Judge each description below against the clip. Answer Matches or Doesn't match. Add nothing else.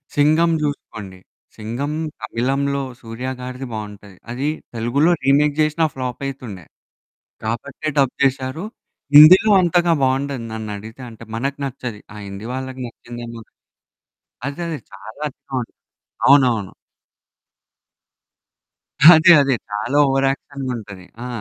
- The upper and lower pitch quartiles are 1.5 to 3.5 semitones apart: Doesn't match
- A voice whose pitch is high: Doesn't match